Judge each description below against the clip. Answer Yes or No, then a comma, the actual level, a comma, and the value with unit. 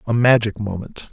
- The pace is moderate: Yes, average, 160 wpm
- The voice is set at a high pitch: No, low, 110 Hz